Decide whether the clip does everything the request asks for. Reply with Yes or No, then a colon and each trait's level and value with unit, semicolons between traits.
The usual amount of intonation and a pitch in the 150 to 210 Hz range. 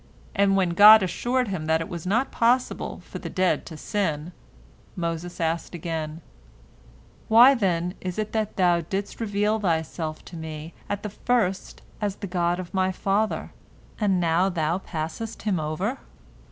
Yes: average, 3.8 semitones; medium, 185 Hz